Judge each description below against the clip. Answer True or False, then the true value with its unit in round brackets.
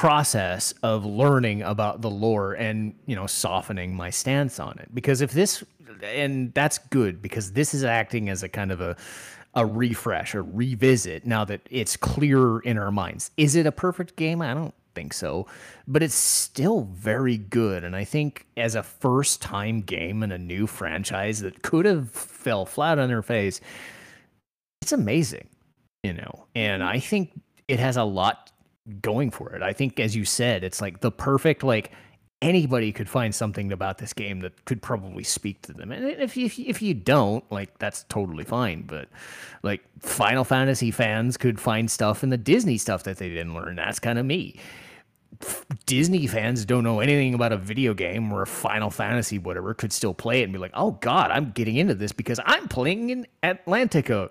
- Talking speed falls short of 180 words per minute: False (190 wpm)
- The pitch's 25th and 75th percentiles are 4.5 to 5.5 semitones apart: True (4.8 semitones)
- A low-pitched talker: True (115 Hz)